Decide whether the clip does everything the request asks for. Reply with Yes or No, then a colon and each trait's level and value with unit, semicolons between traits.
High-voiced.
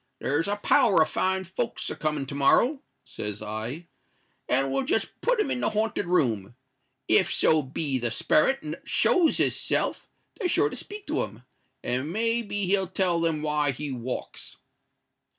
No: medium, 160 Hz